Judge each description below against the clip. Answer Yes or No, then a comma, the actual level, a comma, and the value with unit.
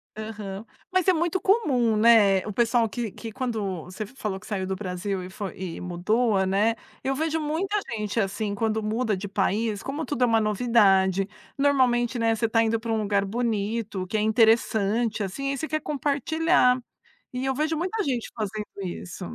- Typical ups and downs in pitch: Yes, average, 4.1 semitones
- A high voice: Yes, high, 225 Hz